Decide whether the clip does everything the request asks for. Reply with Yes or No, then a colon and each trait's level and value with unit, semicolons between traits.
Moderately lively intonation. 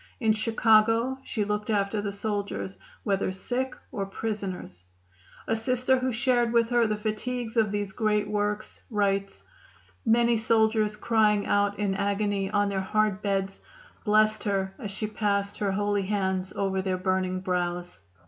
No: narrow, 2.1 semitones